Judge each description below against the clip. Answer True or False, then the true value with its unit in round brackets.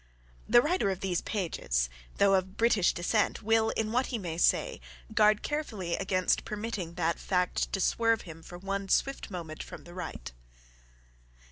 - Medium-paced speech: True (160 wpm)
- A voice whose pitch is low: False (195 Hz)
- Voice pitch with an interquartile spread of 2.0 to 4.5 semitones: True (4.0 semitones)